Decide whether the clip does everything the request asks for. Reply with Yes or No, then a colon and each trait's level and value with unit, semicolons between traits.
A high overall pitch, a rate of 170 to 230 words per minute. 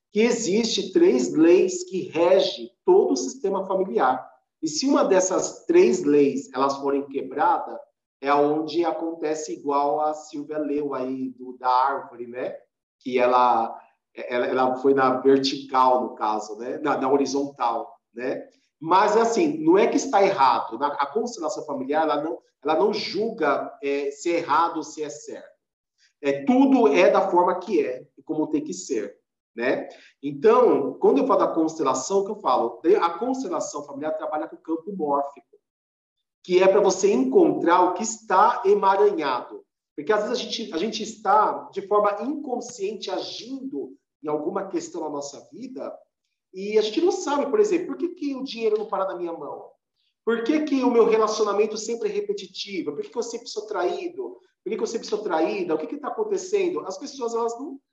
Yes: high, 200 Hz; average, 180 wpm